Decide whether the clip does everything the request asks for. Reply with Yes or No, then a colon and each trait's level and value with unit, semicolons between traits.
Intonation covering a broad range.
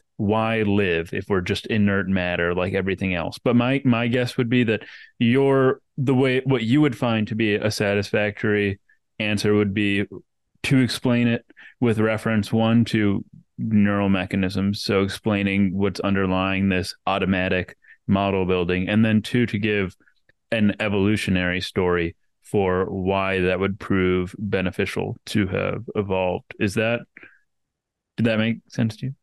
No: average, 2.8 semitones